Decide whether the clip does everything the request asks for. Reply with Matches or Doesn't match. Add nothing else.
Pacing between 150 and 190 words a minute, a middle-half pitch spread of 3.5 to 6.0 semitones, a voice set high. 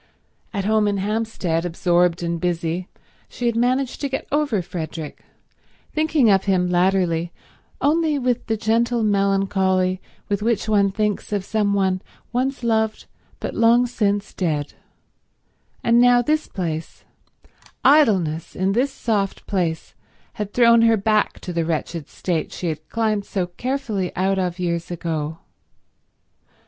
Doesn't match